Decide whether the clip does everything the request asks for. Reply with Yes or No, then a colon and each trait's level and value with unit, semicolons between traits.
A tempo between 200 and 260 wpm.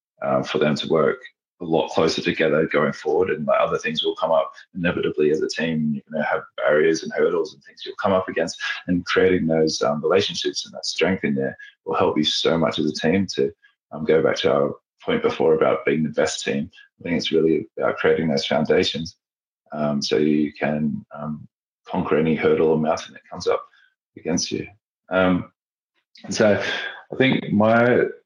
Yes: fast, 205 wpm